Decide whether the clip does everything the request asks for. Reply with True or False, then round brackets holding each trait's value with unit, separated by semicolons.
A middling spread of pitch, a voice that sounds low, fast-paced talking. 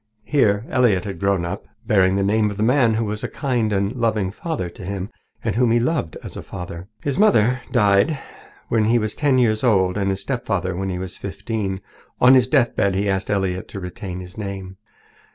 True (3.6 semitones; 105 Hz; 210 wpm)